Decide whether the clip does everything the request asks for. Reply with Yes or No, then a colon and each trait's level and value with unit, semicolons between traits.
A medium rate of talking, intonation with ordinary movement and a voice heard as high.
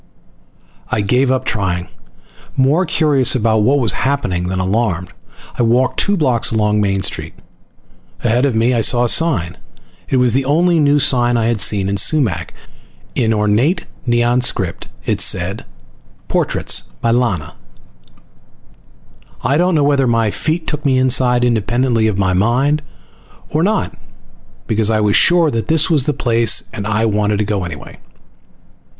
No: average, 160 wpm; average, 4.6 semitones; low, 120 Hz